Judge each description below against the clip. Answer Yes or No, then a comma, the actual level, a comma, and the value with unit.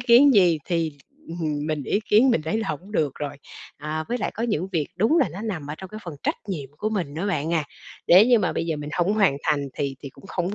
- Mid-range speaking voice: Yes, medium, 175 Hz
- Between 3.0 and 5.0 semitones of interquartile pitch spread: No, wide, 5.6 semitones